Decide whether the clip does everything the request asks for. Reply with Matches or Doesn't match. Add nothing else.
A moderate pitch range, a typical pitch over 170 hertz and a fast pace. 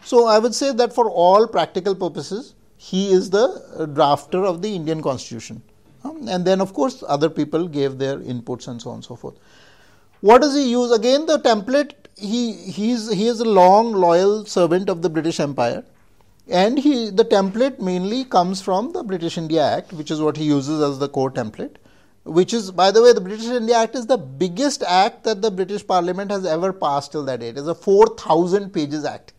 Doesn't match